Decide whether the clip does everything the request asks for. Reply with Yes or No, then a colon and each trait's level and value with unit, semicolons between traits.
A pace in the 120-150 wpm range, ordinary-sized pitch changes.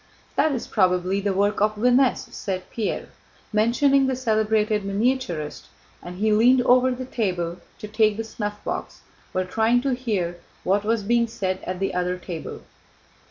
No: average, 160 wpm; average, 4.3 semitones